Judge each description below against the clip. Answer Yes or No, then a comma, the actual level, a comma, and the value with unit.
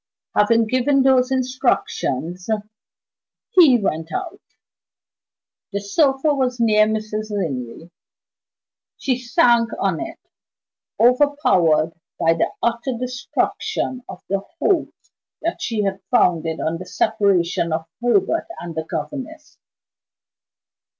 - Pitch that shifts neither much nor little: No, wide, 6.6 semitones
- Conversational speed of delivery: No, slow, 105 wpm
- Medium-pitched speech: No, high, 230 Hz